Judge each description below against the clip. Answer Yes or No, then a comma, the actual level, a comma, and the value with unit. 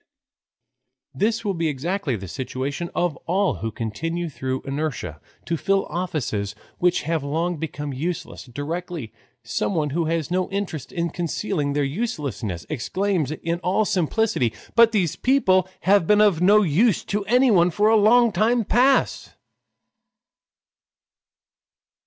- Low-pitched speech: No, medium, 170 Hz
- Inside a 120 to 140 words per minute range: Yes, slow, 135 wpm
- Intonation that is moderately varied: No, wide, 5.9 semitones